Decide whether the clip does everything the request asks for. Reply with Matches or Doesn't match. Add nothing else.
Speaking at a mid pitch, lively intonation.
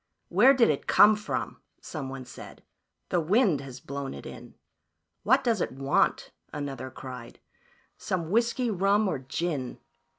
Matches